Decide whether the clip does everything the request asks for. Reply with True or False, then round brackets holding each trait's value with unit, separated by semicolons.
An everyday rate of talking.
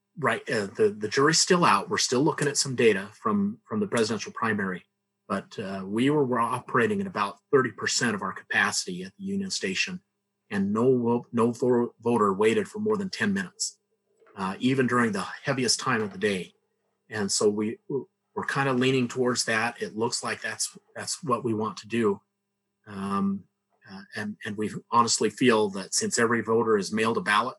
True (185 wpm)